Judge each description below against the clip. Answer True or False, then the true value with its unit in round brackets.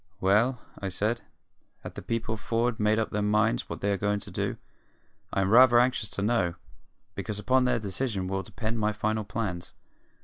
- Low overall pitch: True (110 Hz)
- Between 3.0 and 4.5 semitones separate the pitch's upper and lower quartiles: False (2.5 semitones)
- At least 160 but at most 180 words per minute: False (190 wpm)